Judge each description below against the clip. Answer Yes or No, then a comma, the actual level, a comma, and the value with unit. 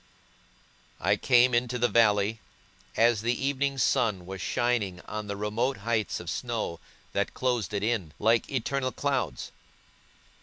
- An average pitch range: Yes, average, 3.4 semitones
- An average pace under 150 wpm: Yes, average, 140 wpm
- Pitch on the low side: Yes, low, 115 Hz